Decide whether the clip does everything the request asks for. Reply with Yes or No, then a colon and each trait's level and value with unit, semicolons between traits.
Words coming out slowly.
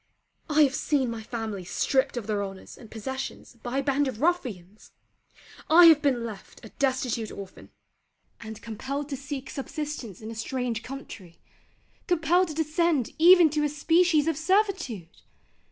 No: average, 155 wpm